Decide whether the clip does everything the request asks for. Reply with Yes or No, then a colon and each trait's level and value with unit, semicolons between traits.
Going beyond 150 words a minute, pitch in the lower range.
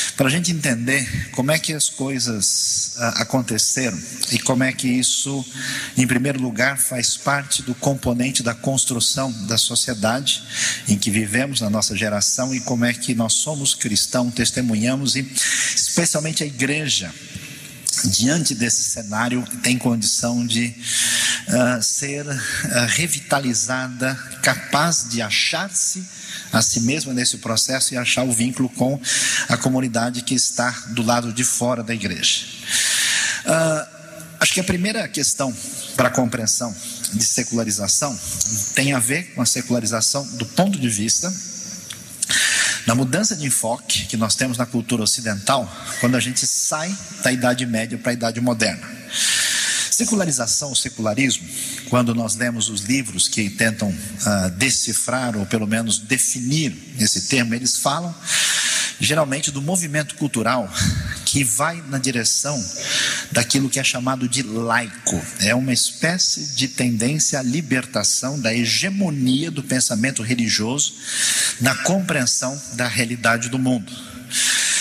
No: average, 135 wpm; low, 125 Hz